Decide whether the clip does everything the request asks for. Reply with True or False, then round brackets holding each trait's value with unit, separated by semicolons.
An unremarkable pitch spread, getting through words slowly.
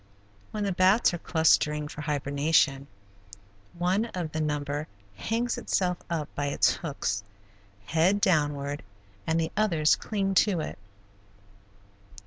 True (4.2 semitones; 120 wpm)